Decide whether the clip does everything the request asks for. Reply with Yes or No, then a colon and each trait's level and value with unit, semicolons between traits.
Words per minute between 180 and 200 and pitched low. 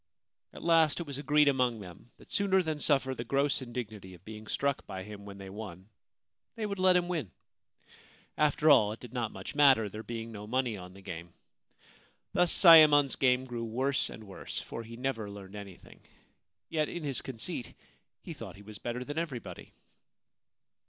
Yes: average, 185 wpm; low, 125 Hz